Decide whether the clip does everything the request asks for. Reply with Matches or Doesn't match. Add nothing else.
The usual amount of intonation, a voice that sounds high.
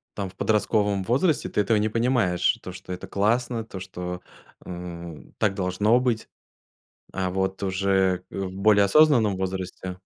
Doesn't match